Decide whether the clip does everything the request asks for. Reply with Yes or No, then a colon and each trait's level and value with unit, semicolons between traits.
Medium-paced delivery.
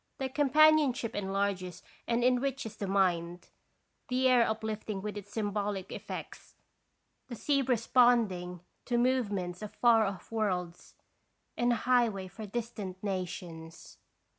No: slow, 120 wpm